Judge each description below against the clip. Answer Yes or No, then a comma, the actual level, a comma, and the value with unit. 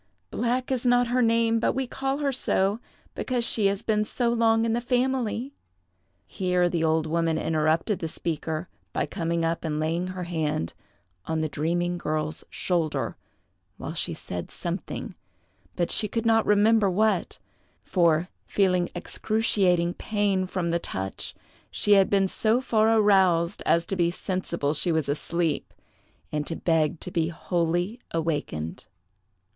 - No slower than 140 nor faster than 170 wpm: Yes, average, 150 wpm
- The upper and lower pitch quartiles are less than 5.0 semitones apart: No, average, 5.3 semitones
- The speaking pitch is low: No, medium, 180 Hz